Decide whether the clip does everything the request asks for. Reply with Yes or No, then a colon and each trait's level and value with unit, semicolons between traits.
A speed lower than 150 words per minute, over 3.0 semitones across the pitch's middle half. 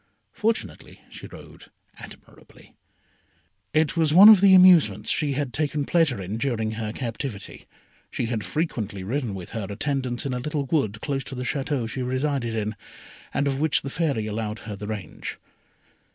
No: average, 165 wpm; wide, 5.4 semitones